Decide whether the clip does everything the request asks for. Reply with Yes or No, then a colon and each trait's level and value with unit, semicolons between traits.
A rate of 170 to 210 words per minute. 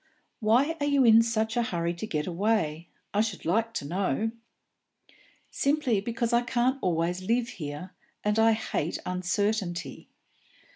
No: average, 145 wpm